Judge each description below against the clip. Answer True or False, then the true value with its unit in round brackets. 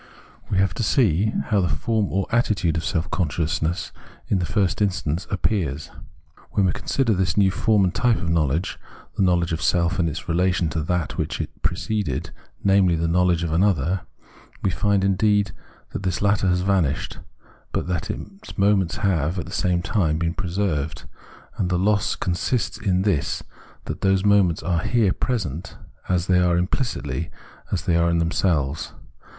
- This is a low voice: True (90 Hz)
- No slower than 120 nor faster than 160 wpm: False (175 wpm)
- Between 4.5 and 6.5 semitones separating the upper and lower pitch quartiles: False (3.0 semitones)